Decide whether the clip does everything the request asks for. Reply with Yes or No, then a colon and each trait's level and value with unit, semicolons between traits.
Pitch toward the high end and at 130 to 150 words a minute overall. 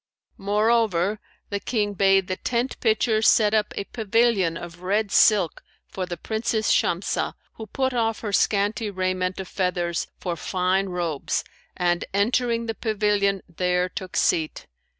Yes: high, 200 Hz; average, 145 wpm